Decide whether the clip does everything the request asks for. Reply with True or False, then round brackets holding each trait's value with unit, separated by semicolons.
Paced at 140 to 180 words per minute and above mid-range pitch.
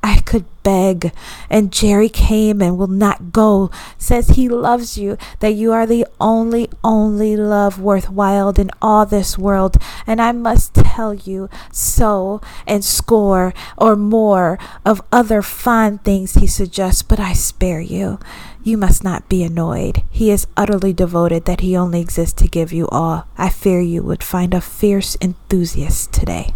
True (165 wpm; 200 Hz)